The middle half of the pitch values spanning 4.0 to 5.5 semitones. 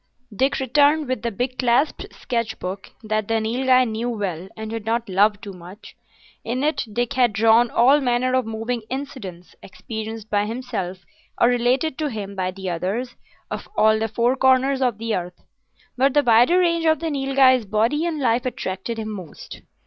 No: average, 3.5 semitones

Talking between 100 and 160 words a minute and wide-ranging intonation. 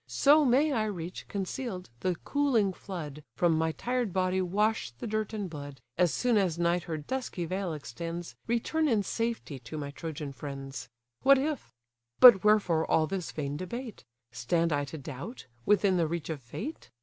No: average, 170 wpm; wide, 6.2 semitones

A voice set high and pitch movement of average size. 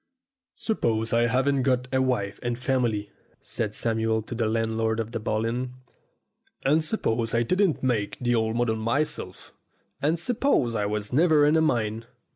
No: low, 120 Hz; average, 3.1 semitones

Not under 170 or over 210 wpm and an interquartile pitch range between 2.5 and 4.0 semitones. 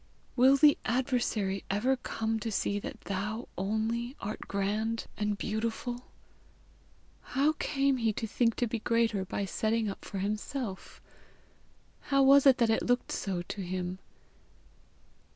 No: average, 140 wpm; average, 3.4 semitones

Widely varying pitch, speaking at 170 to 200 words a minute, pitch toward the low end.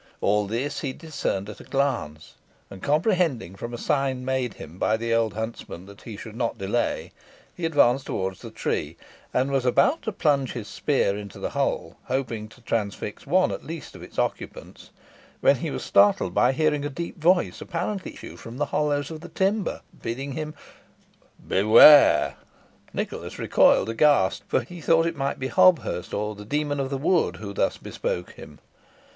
Yes: wide, 5.9 semitones; average, 180 wpm; low, 130 Hz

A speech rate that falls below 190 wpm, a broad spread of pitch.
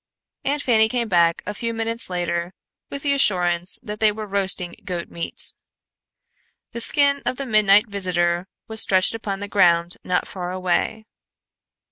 No: average, 155 wpm; average, 4.1 semitones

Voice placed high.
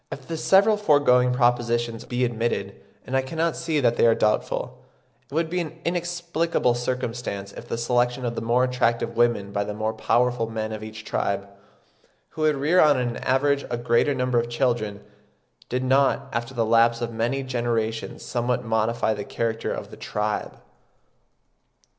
No: low, 120 Hz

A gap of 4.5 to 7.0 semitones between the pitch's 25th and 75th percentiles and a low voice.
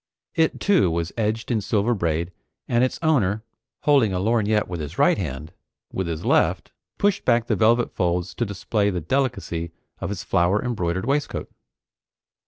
Yes: average, 5.3 semitones; low, 105 Hz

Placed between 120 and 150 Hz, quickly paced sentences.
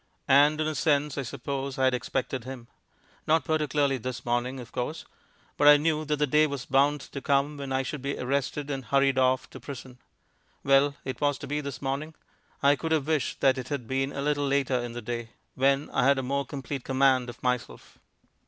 Yes: medium, 140 Hz; fast, 210 wpm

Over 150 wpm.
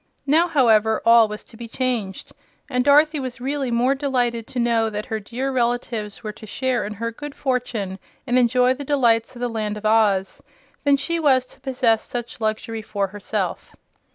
Yes: average, 185 wpm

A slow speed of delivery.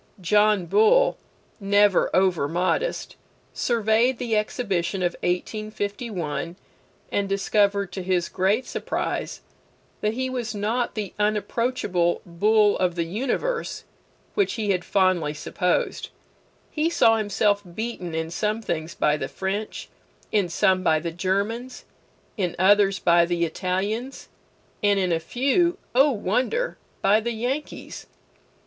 Yes: slow, 125 wpm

